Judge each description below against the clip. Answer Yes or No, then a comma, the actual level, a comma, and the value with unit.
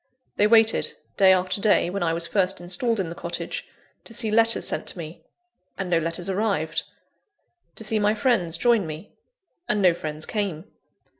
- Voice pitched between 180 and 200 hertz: Yes, high, 190 Hz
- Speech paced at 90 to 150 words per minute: No, average, 175 wpm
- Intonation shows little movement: No, average, 4.0 semitones